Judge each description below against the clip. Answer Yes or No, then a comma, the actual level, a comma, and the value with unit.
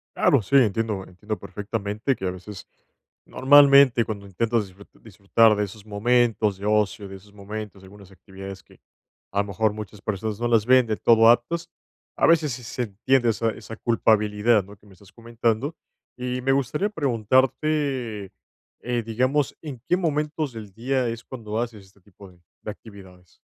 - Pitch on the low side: Yes, low, 110 Hz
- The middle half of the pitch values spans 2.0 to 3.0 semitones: No, average, 3.6 semitones